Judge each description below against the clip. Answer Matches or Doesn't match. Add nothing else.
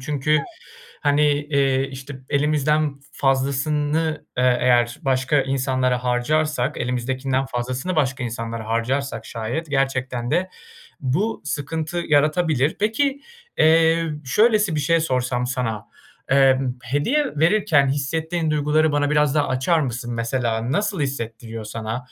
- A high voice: Doesn't match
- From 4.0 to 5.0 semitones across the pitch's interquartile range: Doesn't match